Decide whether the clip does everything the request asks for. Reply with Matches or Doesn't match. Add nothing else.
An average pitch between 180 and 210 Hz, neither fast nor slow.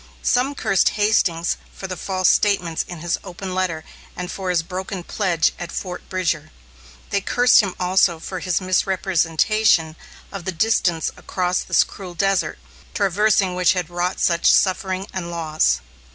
Matches